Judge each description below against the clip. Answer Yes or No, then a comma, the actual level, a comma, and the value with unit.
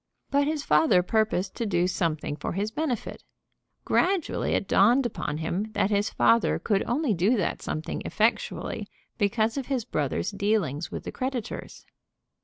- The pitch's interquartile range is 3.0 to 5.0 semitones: No, wide, 5.4 semitones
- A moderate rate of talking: Yes, average, 155 wpm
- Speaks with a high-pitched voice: Yes, high, 210 Hz